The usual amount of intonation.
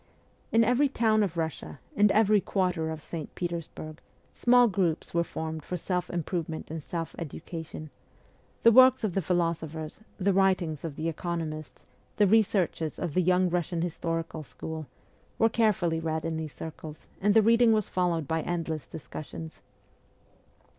Yes: average, 3.6 semitones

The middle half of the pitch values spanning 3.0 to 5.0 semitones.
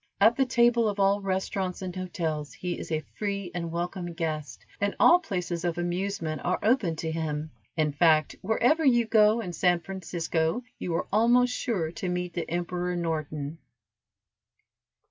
Yes: average, 3.7 semitones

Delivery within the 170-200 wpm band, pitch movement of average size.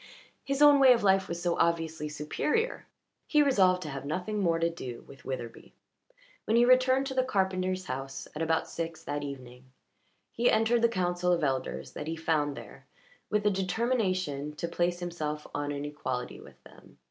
No: average, 180 wpm; wide, 6.2 semitones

